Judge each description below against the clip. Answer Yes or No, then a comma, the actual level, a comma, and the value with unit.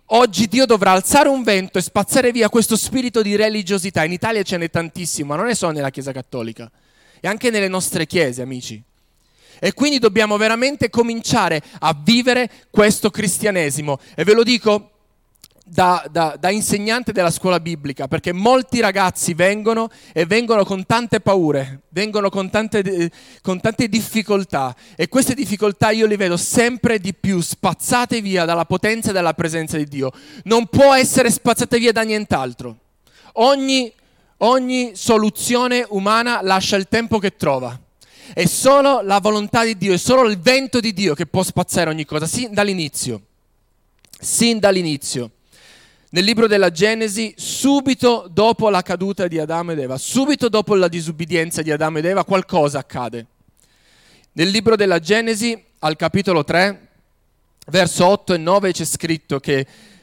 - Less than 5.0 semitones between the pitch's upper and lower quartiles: No, wide, 5.4 semitones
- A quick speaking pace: No, average, 160 wpm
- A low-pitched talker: No, high, 195 Hz